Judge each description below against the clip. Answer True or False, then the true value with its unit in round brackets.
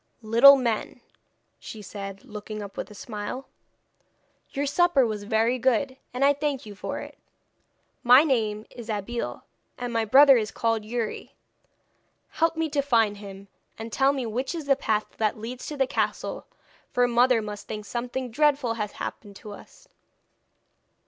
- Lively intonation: False (4.0 semitones)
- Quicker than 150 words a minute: True (160 wpm)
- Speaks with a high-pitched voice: True (235 Hz)